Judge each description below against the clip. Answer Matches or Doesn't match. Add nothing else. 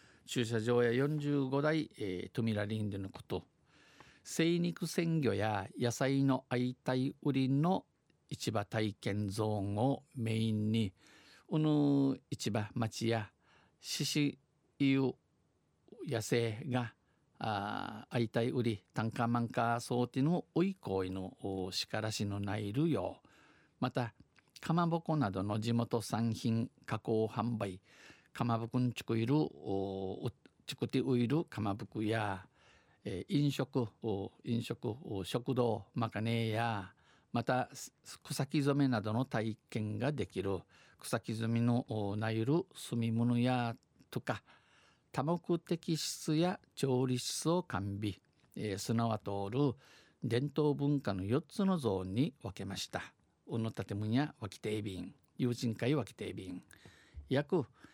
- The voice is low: Matches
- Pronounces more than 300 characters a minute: Doesn't match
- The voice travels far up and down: Doesn't match